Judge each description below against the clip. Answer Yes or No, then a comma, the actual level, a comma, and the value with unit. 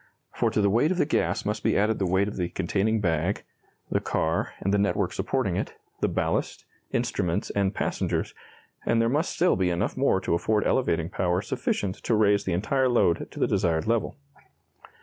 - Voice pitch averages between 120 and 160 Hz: No, low, 100 Hz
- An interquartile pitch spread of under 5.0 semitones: Yes, average, 4.3 semitones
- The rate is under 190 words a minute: No, average, 195 wpm